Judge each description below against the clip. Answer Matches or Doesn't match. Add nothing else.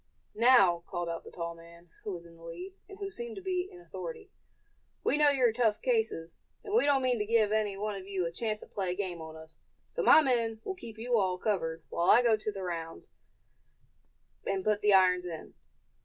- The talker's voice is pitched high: Matches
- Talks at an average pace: Doesn't match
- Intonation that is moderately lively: Doesn't match